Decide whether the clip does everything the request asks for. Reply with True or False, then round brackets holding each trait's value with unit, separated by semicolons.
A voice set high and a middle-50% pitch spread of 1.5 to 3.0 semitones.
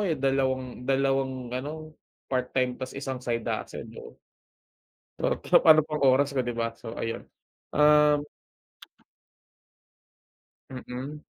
False (135 Hz; 2.5 semitones)